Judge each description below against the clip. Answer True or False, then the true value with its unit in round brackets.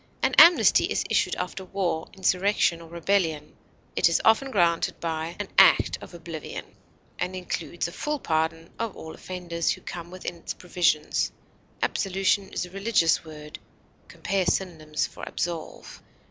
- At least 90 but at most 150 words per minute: True (145 wpm)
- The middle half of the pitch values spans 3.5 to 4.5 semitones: False (2.7 semitones)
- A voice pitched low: False (175 Hz)